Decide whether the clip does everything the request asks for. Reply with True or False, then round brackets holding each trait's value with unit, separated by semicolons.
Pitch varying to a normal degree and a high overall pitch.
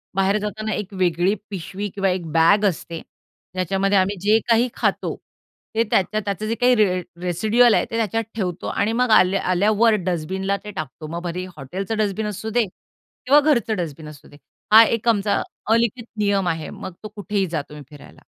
True (3.4 semitones; 200 Hz)